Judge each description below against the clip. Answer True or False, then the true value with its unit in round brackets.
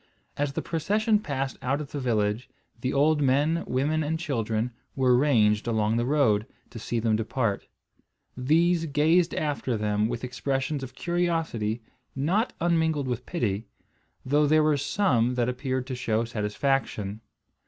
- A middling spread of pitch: True (4.8 semitones)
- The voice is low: True (130 Hz)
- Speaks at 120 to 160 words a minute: True (150 wpm)